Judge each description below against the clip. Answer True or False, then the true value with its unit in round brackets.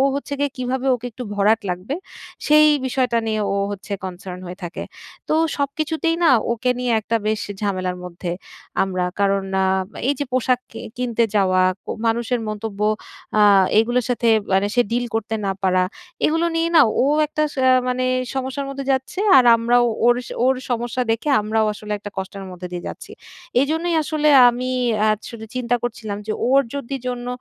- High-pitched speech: True (235 Hz)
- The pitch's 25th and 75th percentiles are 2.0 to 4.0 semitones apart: False (4.4 semitones)